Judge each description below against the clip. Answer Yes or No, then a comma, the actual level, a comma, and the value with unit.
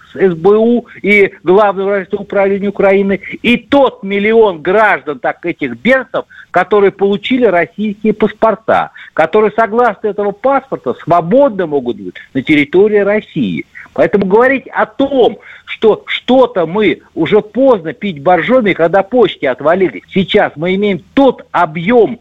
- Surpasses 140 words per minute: No, average, 120 wpm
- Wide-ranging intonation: No, average, 3.7 semitones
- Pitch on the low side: No, high, 205 Hz